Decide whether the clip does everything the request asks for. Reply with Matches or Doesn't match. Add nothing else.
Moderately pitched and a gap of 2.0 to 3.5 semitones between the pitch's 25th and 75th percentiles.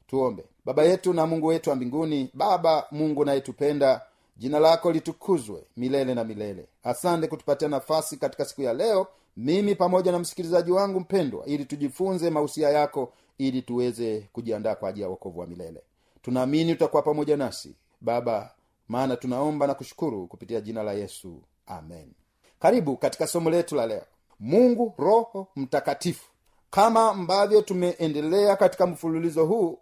Doesn't match